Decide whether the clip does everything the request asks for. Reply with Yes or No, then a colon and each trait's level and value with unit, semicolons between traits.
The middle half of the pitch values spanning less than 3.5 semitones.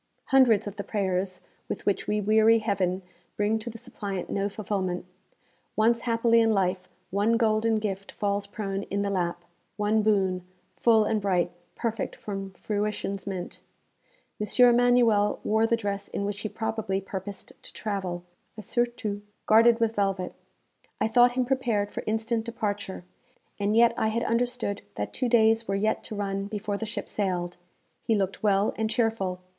Yes: narrow, 2.4 semitones